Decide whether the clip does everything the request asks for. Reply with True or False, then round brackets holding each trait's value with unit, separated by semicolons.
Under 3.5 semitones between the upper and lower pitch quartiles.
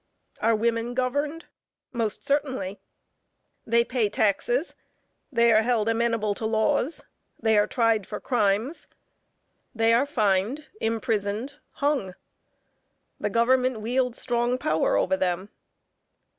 True (3.1 semitones)